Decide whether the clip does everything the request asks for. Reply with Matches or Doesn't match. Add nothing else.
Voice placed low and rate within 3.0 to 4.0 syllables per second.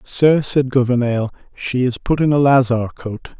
Doesn't match